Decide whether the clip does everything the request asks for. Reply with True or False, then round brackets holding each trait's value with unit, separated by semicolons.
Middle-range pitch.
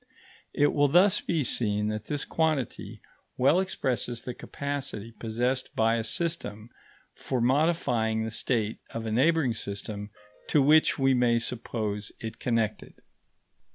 False (120 Hz)